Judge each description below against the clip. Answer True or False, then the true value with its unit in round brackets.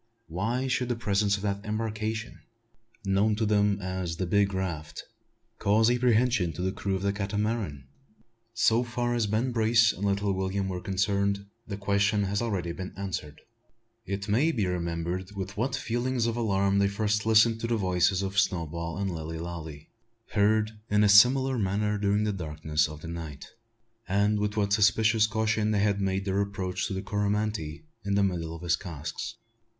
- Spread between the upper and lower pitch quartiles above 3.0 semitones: False (2.6 semitones)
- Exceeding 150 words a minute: True (175 wpm)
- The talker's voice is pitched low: True (100 Hz)